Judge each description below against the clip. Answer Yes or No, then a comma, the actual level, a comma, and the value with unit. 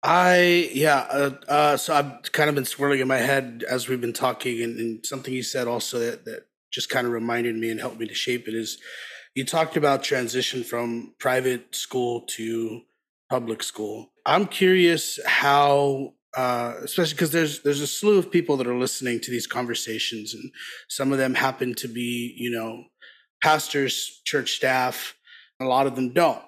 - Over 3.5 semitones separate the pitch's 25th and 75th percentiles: No, average, 3.1 semitones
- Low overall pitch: Yes, low, 130 Hz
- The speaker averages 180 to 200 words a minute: Yes, average, 190 wpm